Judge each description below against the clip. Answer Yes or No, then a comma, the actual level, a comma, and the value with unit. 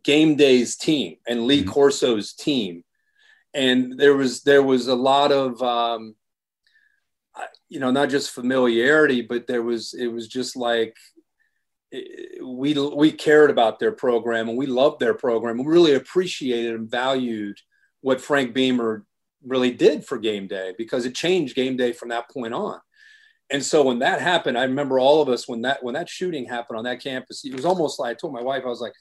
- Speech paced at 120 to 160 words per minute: No, average, 190 wpm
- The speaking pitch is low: Yes, low, 130 Hz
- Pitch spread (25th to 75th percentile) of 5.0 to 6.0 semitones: No, average, 4.0 semitones